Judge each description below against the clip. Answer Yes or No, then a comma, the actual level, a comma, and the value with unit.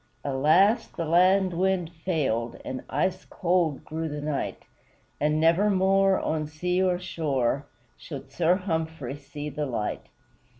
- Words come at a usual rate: No, slow, 130 wpm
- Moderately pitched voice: Yes, medium, 160 Hz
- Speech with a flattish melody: No, average, 3.9 semitones